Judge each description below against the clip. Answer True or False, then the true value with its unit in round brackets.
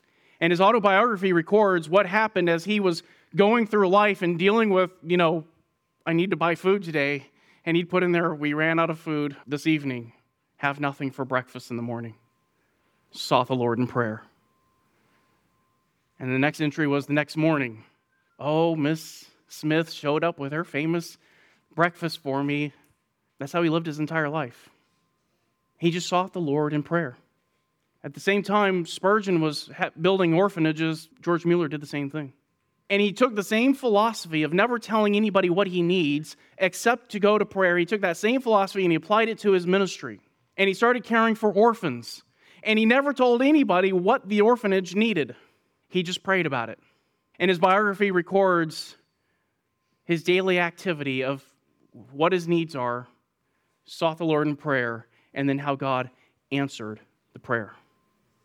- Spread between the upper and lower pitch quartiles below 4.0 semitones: False (5.0 semitones)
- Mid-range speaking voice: True (170 Hz)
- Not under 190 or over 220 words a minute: False (170 wpm)